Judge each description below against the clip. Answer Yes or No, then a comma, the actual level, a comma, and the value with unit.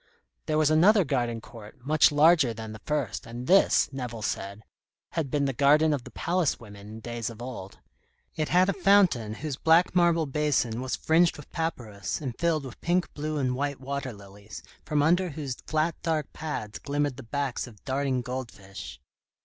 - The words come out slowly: No, average, 180 wpm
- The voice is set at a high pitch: No, medium, 140 Hz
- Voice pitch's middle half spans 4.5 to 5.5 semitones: Yes, average, 5.1 semitones